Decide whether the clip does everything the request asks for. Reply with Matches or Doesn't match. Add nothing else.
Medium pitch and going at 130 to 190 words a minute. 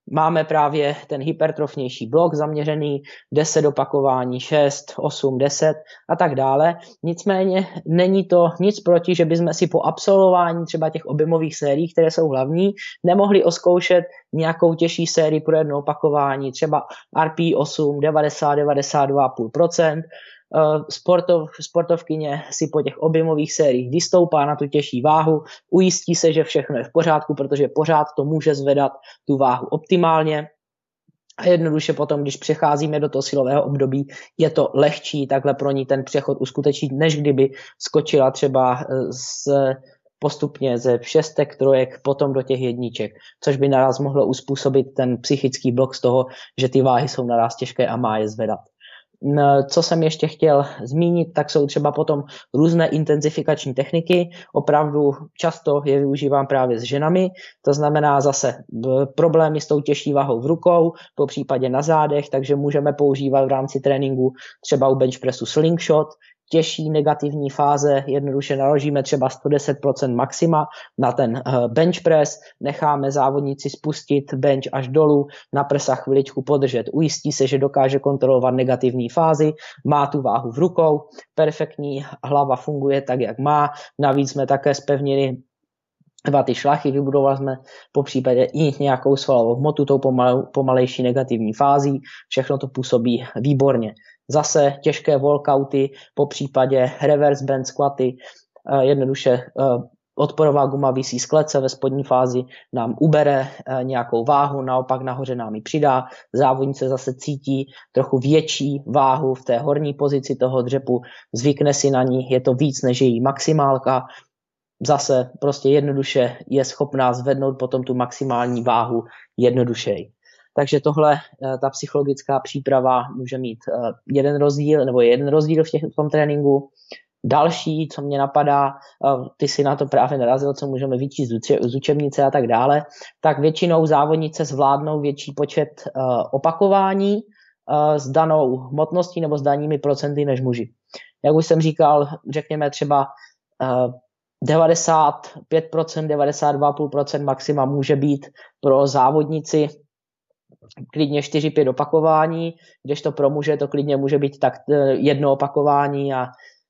Matches